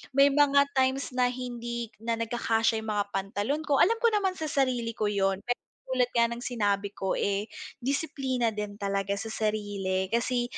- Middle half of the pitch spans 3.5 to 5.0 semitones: Yes, average, 4.1 semitones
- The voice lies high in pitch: Yes, high, 235 Hz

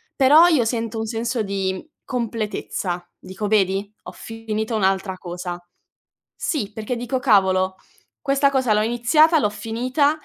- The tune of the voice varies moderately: Yes, average, 4.3 semitones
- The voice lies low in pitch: No, high, 220 Hz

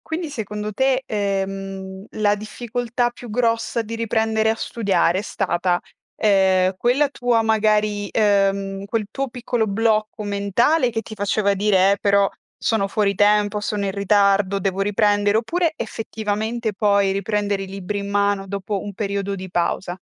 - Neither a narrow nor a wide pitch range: No, narrow, 2.1 semitones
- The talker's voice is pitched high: Yes, high, 205 Hz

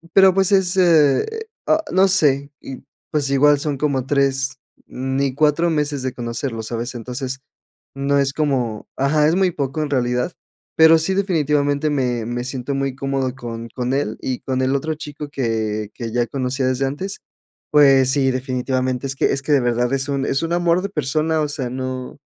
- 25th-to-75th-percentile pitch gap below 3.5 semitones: Yes, average, 2.9 semitones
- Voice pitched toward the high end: No, low, 135 Hz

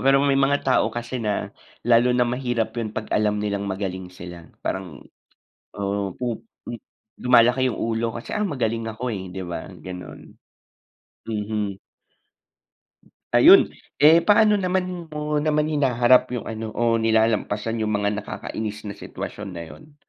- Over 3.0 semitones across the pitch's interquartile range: Yes, average, 4.5 semitones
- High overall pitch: No, low, 115 Hz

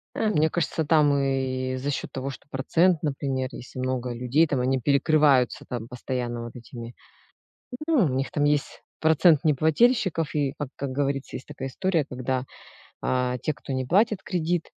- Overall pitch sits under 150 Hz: Yes, medium, 140 Hz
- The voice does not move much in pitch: No, average, 3.4 semitones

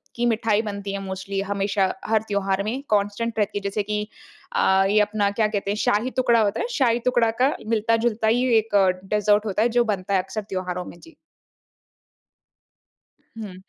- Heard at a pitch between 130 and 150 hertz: No, high, 210 Hz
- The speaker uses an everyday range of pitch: No, narrow, 2.3 semitones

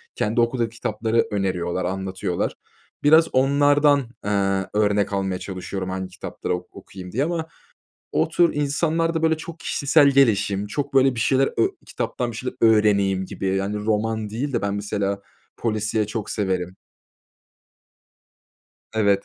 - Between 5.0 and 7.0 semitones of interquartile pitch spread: Yes, wide, 5.6 semitones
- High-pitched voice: No, low, 105 Hz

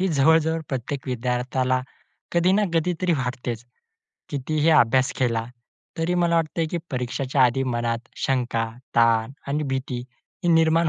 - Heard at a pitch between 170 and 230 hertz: No, low, 135 Hz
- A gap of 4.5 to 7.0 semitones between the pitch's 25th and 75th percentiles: Yes, average, 4.8 semitones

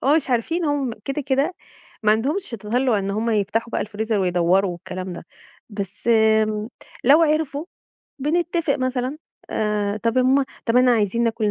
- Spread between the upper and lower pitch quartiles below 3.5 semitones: No, average, 4.6 semitones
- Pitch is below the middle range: No, high, 230 Hz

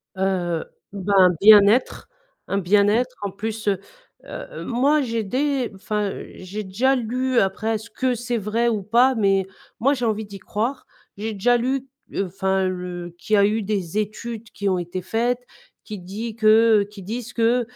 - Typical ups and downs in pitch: Yes, average, 3.6 semitones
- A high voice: Yes, high, 215 Hz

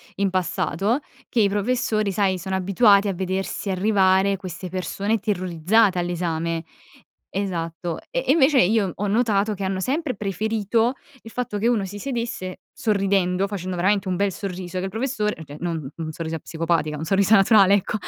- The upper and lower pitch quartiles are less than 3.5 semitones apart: Yes, average, 2.8 semitones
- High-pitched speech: Yes, high, 195 Hz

